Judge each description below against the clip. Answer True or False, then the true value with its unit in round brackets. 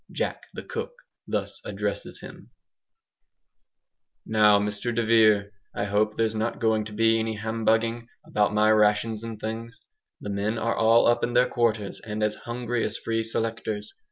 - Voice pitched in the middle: False (110 Hz)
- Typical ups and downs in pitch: False (1.3 semitones)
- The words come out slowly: False (160 wpm)